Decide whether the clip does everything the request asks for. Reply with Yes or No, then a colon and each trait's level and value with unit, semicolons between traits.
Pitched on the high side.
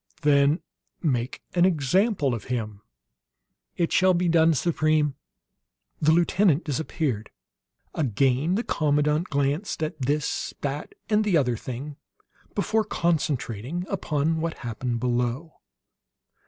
No: medium, 150 Hz